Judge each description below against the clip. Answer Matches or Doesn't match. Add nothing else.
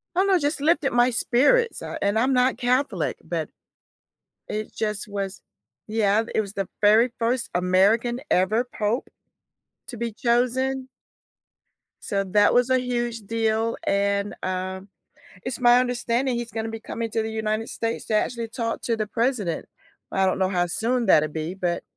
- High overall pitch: Matches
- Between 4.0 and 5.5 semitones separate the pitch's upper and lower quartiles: Doesn't match